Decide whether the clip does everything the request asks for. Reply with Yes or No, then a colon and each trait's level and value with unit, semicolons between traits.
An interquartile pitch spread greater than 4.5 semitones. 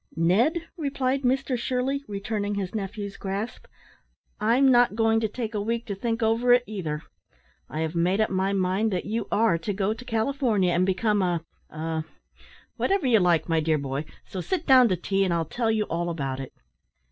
Yes: average, 4.9 semitones